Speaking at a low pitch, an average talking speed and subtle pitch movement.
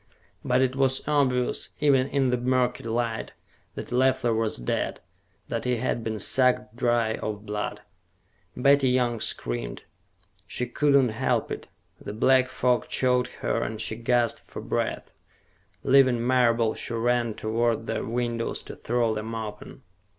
Yes: low, 120 Hz; average, 150 wpm; narrow, 2.3 semitones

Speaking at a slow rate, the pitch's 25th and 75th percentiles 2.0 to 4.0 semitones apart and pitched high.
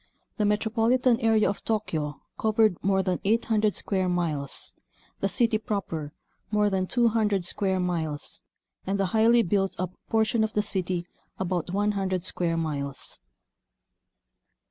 Yes: slow, 130 wpm; average, 3.6 semitones; high, 195 Hz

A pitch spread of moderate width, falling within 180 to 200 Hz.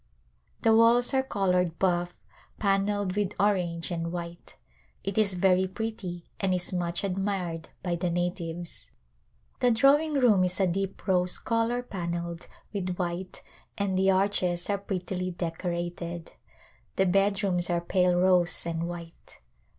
No: narrow, 2.3 semitones; medium, 185 Hz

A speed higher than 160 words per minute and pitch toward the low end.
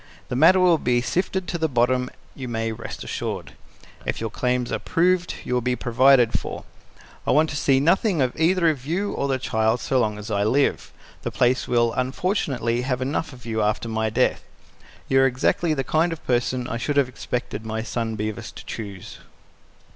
Yes: average, 195 wpm; low, 125 Hz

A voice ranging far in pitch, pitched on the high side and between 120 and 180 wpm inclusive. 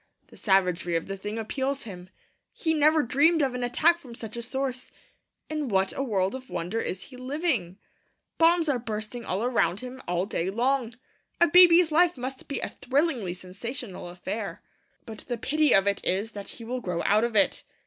No: wide, 5.9 semitones; high, 240 Hz; average, 190 wpm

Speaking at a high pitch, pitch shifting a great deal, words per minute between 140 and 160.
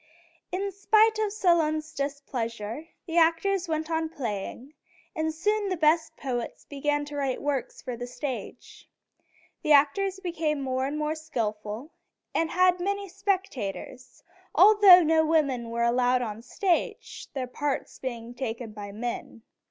Yes: very high, 300 Hz; wide, 5.8 semitones; average, 145 wpm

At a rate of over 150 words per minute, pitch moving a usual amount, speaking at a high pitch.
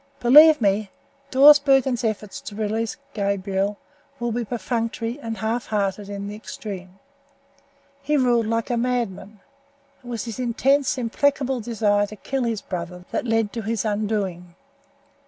No: slow, 135 wpm; average, 3.1 semitones; high, 225 Hz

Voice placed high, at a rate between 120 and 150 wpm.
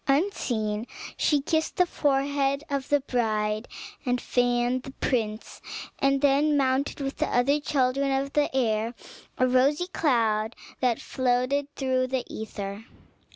Yes: very high, 260 Hz; average, 140 wpm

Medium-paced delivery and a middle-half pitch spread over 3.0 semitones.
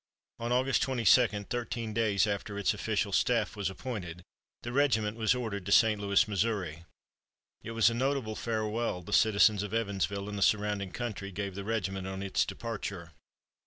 No: average, 165 wpm; narrow, 2.6 semitones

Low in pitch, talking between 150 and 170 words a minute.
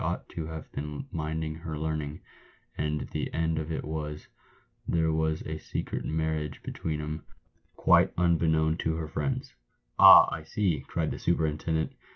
Yes: very low, 80 Hz; average, 160 wpm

